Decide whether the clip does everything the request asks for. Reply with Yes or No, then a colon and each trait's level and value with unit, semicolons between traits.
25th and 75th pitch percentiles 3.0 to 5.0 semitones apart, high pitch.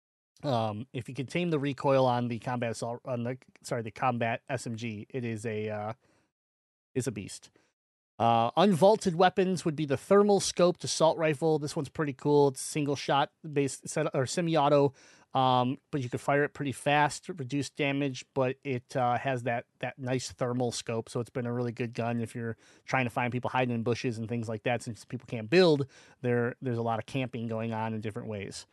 No: average, 3.6 semitones; low, 130 Hz